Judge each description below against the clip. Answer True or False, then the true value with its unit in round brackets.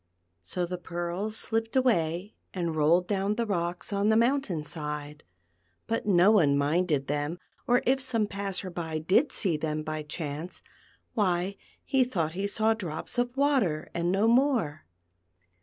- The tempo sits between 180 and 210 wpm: False (155 wpm)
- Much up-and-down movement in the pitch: True (5.7 semitones)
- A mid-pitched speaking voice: True (180 Hz)